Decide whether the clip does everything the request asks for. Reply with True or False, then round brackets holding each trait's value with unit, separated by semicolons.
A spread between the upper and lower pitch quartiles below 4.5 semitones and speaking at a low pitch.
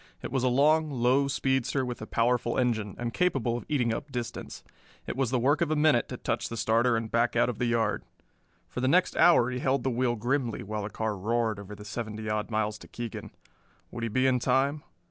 True (2.9 semitones; 120 Hz)